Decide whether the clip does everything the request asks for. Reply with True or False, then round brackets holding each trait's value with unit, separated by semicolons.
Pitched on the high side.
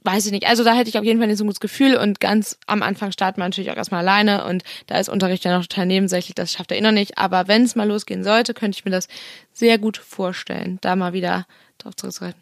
True (200 Hz)